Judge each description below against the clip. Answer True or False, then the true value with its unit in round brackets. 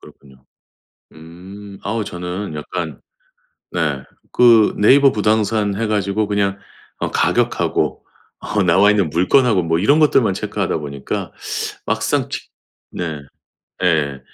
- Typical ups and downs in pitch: True (4.5 semitones)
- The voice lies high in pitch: False (100 Hz)